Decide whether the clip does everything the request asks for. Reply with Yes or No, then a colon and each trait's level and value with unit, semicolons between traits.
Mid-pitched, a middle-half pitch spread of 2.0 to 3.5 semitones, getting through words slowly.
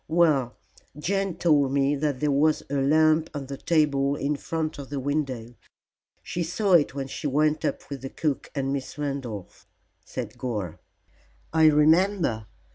No: medium, 145 Hz; narrow, 2.4 semitones; average, 150 wpm